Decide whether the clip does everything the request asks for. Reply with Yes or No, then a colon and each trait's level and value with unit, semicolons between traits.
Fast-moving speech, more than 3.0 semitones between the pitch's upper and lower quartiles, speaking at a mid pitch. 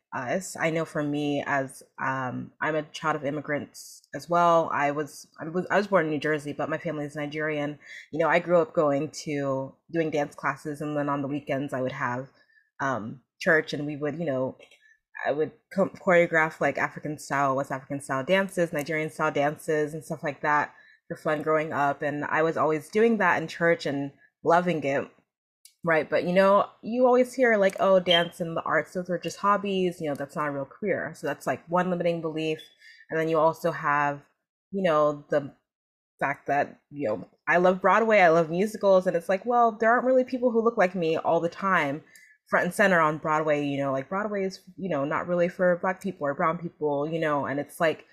Yes: fast, 215 wpm; average, 3.8 semitones; medium, 160 Hz